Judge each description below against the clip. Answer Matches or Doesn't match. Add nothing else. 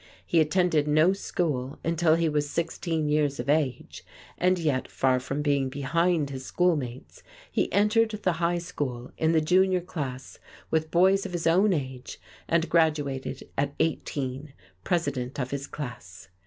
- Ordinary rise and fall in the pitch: Matches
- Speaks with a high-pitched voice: Doesn't match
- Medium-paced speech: Matches